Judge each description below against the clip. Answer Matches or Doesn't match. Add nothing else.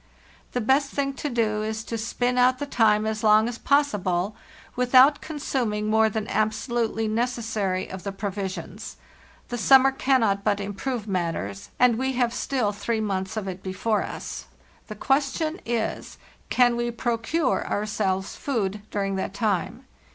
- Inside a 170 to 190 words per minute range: Doesn't match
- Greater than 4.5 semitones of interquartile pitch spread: Doesn't match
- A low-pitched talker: Doesn't match